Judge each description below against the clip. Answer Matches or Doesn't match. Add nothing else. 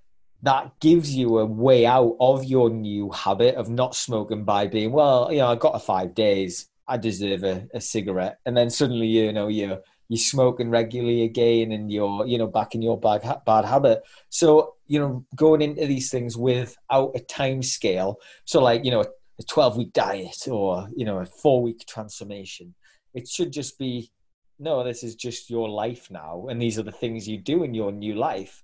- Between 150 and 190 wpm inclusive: Doesn't match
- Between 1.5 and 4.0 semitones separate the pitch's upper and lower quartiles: Matches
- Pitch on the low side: Matches